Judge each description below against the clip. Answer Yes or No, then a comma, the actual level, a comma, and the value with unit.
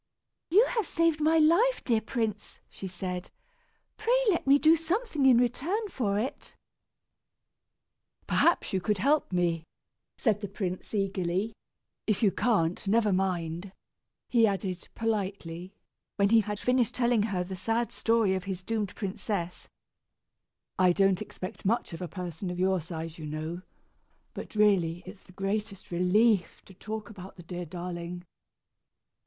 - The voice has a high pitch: Yes, high, 200 Hz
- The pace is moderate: Yes, average, 150 wpm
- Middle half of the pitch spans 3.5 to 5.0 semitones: Yes, average, 4.2 semitones